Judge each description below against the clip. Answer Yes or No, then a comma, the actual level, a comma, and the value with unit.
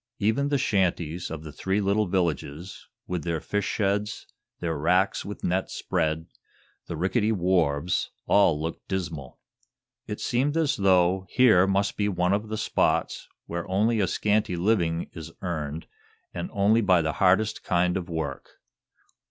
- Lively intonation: No, average, 3.6 semitones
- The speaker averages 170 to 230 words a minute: No, average, 150 wpm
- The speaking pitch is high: No, very low, 95 Hz